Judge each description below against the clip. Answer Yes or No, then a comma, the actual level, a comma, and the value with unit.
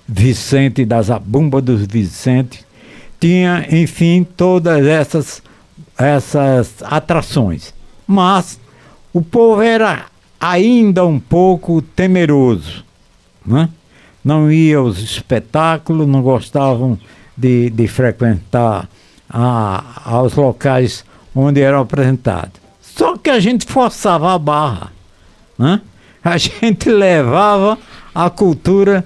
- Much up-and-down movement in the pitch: Yes, wide, 7.1 semitones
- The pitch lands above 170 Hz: No, medium, 140 Hz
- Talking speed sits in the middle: No, slow, 95 wpm